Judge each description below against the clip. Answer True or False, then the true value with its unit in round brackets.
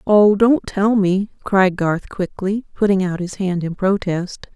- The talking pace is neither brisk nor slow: True (170 wpm)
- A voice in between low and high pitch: False (195 Hz)